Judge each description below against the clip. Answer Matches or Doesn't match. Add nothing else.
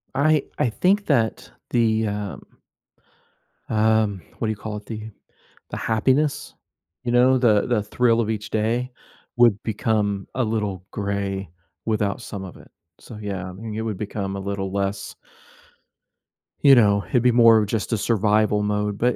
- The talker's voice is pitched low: Matches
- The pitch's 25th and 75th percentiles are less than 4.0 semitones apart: Matches